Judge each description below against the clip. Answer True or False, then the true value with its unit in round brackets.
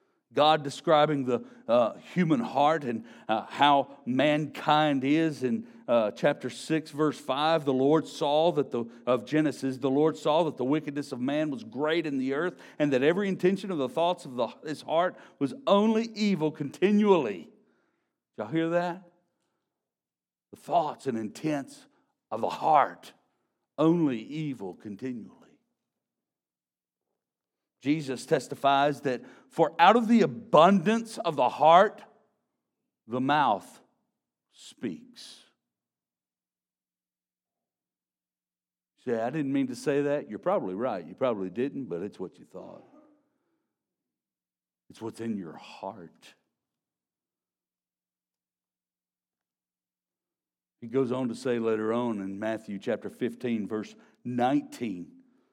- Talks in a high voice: False (140 Hz)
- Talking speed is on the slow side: True (125 wpm)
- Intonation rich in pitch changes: True (7.9 semitones)